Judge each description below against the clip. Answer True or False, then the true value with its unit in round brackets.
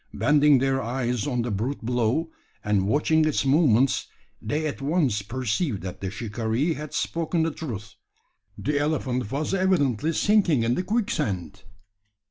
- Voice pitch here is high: False (135 Hz)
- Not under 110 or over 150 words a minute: True (145 wpm)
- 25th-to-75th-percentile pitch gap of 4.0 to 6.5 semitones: True (5.5 semitones)